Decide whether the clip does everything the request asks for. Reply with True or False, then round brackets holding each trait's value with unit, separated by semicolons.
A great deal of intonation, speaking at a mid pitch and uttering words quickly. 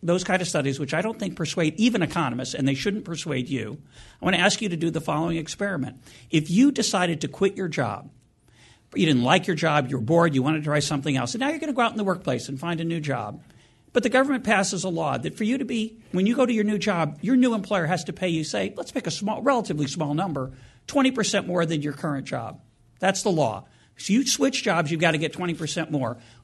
True (6.1 semitones; 165 Hz; 260 wpm)